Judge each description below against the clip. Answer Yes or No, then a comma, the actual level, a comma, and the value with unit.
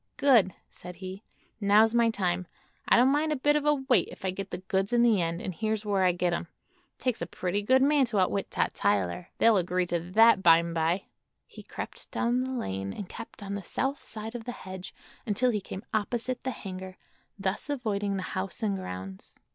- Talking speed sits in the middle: No, fast, 210 wpm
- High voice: Yes, high, 200 Hz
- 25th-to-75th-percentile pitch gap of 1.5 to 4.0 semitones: No, average, 4.5 semitones